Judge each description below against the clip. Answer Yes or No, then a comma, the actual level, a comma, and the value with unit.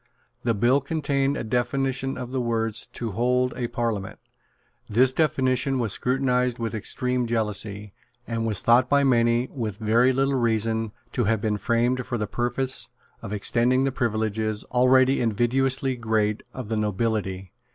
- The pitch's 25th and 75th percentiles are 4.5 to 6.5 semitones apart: No, narrow, 2.6 semitones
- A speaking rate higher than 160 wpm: No, average, 150 wpm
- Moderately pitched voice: No, low, 120 Hz